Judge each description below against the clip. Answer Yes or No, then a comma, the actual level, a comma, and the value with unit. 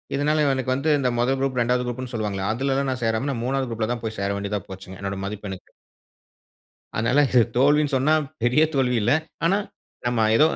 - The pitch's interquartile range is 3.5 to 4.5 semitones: Yes, average, 3.8 semitones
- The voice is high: No, low, 125 Hz